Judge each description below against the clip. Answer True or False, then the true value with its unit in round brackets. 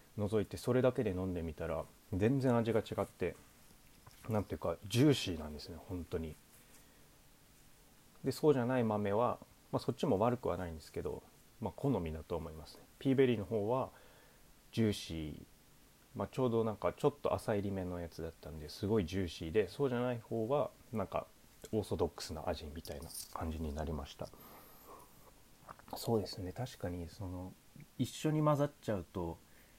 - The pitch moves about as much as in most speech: False (6.3 semitones)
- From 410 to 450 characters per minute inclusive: False (350 characters per minute)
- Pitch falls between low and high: False (95 Hz)